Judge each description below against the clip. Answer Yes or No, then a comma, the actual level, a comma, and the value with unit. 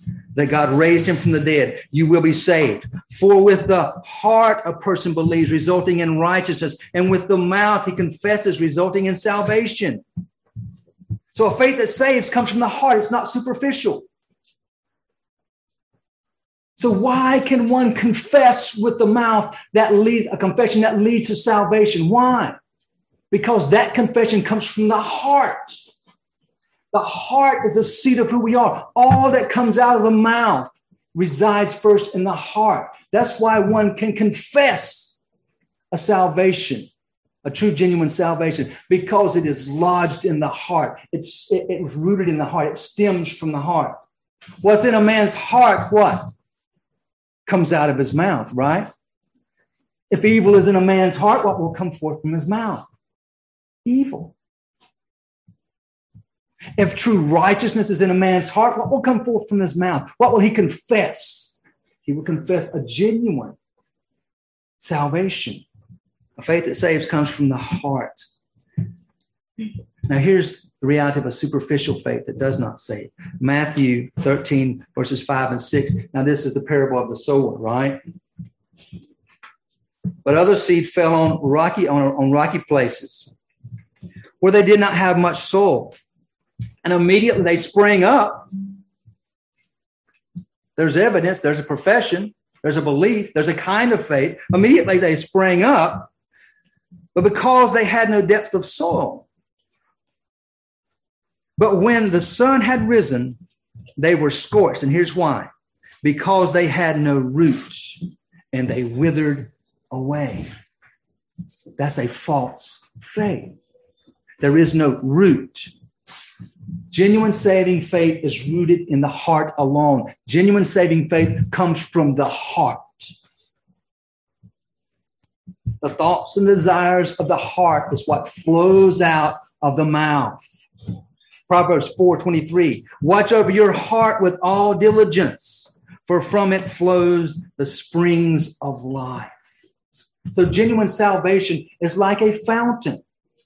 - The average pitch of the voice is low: No, medium, 180 Hz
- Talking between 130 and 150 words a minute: Yes, average, 140 wpm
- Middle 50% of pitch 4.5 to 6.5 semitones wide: Yes, wide, 5.5 semitones